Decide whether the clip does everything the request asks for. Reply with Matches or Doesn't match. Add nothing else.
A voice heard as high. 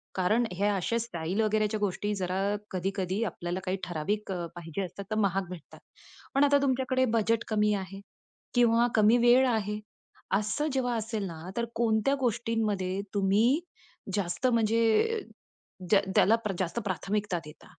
Matches